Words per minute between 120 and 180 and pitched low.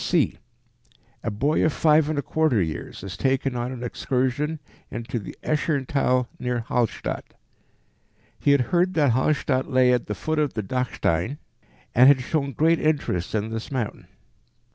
Yes: average, 160 wpm; low, 130 Hz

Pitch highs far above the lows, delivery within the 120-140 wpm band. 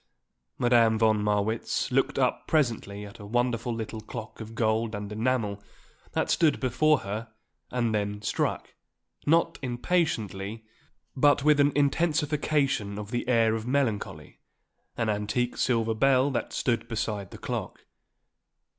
No: average, 3.8 semitones; slow, 135 wpm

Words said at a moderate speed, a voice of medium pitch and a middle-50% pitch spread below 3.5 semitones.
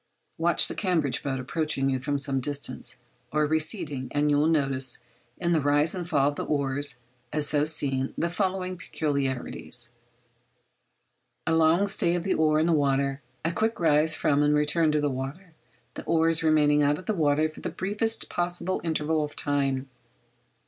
Yes: average, 175 wpm; medium, 150 Hz; average, 2.8 semitones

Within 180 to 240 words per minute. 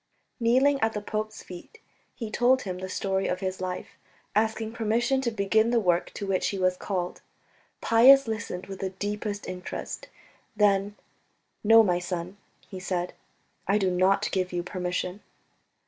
No: average, 160 wpm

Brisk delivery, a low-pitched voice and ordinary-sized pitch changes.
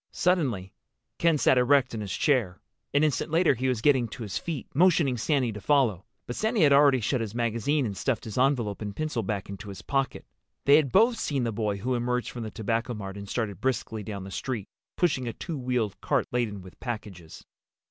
Yes: fast, 210 wpm; low, 120 Hz; average, 5.0 semitones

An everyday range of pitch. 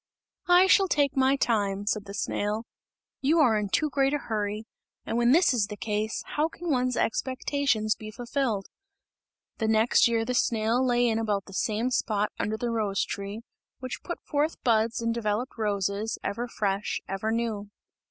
Yes: average, 3.5 semitones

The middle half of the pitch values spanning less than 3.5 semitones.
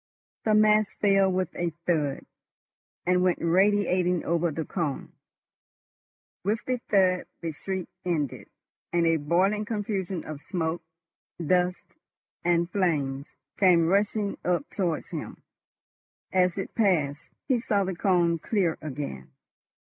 Yes: average, 3.1 semitones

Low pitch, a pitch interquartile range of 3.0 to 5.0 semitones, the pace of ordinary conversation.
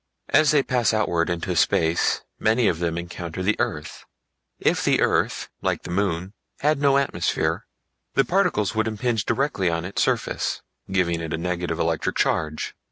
No: very low, 95 Hz; wide, 5.5 semitones; average, 165 wpm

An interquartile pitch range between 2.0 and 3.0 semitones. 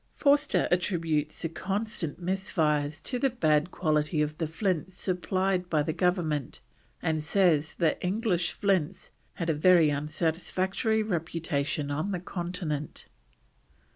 No: average, 3.6 semitones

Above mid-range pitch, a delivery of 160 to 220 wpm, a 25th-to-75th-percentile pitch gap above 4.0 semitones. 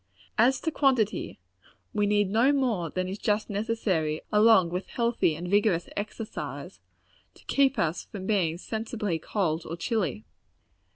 No: high, 205 Hz; average, 140 wpm; average, 4.4 semitones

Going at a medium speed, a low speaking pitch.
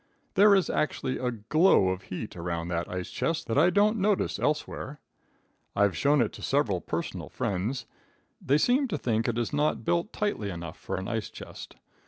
Yes: average, 185 wpm; low, 130 Hz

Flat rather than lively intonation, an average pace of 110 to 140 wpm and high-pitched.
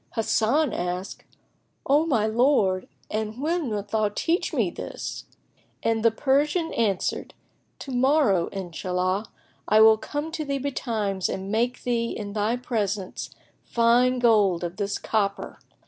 No: average, 4.5 semitones; slow, 135 wpm; high, 220 Hz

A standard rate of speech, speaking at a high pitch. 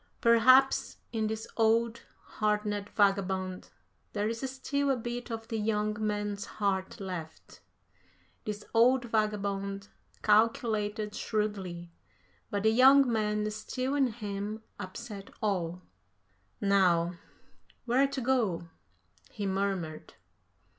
No: slow, 105 wpm; high, 210 Hz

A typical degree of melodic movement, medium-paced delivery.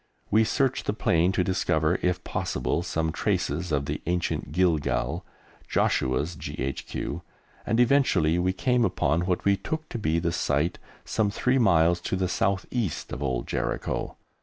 Yes: average, 4.2 semitones; average, 160 wpm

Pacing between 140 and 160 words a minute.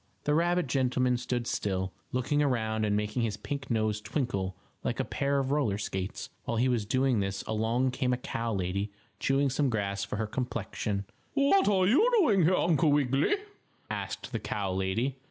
No: average, 180 wpm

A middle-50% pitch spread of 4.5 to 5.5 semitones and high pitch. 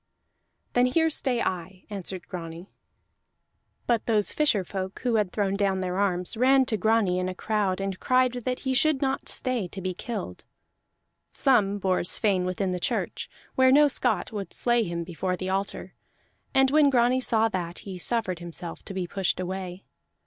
Yes: average, 5.0 semitones; high, 200 Hz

